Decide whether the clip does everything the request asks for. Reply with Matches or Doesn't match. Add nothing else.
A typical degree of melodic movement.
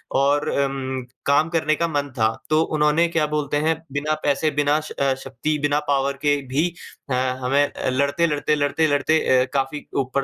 Doesn't match